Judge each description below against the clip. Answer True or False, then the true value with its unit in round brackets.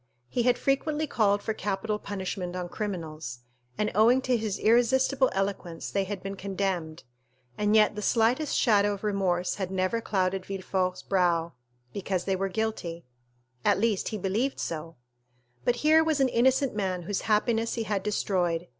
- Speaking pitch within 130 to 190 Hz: False (200 Hz)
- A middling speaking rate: True (165 wpm)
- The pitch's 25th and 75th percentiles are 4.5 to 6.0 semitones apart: False (3.6 semitones)